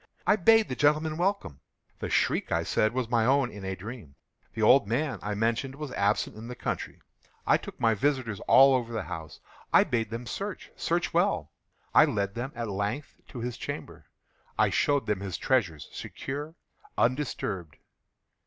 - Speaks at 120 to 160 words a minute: No, average, 170 wpm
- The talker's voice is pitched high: No, low, 120 Hz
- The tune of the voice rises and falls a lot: No, average, 4.8 semitones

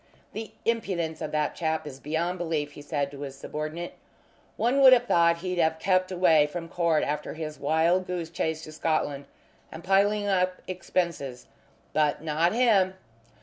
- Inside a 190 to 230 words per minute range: No, average, 165 wpm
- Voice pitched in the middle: Yes, medium, 165 Hz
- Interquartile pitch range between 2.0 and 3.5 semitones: Yes, average, 3.2 semitones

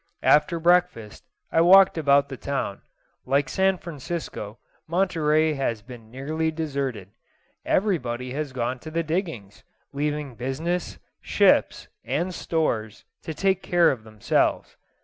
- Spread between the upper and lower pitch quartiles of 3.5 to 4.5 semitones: No, average, 5.0 semitones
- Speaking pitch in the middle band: Yes, medium, 150 Hz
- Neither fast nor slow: No, slow, 125 wpm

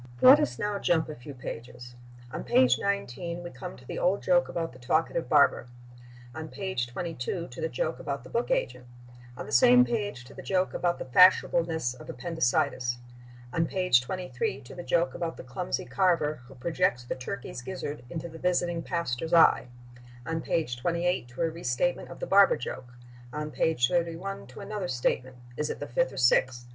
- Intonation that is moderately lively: No, wide, 6.3 semitones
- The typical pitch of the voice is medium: Yes, medium, 165 Hz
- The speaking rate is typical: Yes, average, 185 wpm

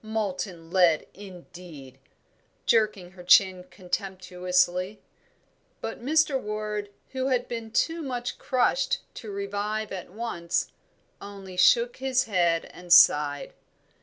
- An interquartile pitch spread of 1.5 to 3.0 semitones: No, average, 4.2 semitones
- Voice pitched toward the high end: Yes, high, 200 Hz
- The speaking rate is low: Yes, slow, 110 wpm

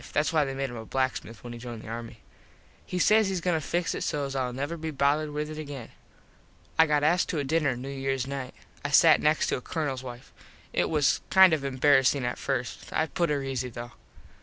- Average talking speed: No, fast, 230 wpm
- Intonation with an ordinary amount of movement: Yes, average, 3.2 semitones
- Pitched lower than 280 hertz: Yes, medium, 140 Hz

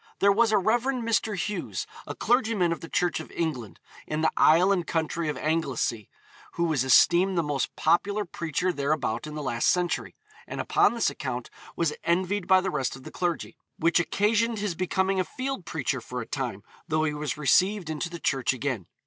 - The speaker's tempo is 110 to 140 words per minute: No, average, 195 wpm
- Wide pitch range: No, average, 4.6 semitones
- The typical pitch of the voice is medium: Yes, medium, 170 Hz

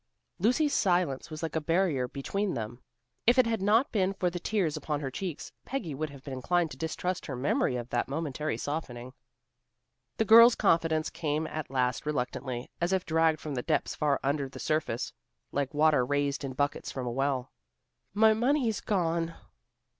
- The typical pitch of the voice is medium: Yes, medium, 155 Hz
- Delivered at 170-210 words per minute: Yes, average, 175 wpm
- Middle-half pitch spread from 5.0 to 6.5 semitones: Yes, average, 5.3 semitones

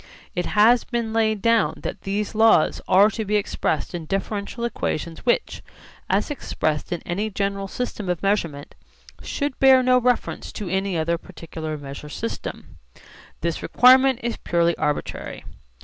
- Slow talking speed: No, average, 150 wpm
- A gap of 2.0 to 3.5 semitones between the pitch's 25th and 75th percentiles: No, average, 5.3 semitones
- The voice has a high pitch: Yes, high, 200 Hz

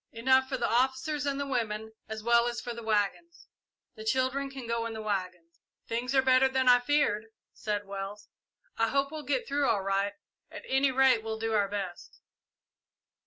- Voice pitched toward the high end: Yes, high, 235 Hz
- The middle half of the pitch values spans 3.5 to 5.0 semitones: Yes, average, 3.8 semitones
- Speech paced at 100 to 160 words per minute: No, average, 190 wpm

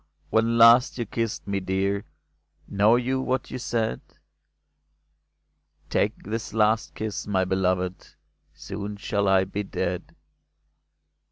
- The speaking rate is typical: No, slow, 120 wpm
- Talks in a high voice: No, low, 105 Hz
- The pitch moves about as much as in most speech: Yes, average, 3.0 semitones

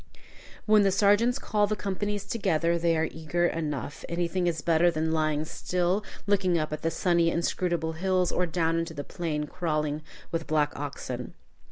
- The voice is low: No, medium, 170 Hz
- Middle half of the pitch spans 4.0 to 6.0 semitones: No, average, 2.9 semitones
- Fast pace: No, average, 170 wpm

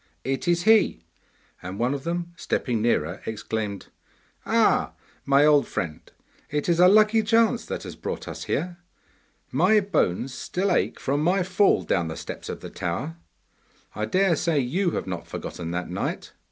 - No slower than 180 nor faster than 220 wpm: No, average, 165 wpm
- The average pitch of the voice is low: No, medium, 150 Hz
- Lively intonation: Yes, wide, 9.0 semitones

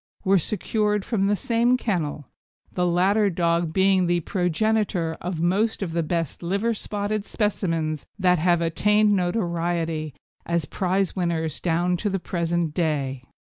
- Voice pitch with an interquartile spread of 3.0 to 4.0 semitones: Yes, average, 3.5 semitones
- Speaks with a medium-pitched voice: Yes, medium, 180 Hz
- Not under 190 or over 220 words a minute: No, average, 140 wpm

